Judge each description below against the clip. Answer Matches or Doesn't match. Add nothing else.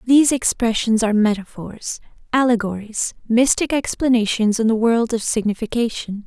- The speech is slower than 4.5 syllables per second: Doesn't match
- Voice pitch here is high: Matches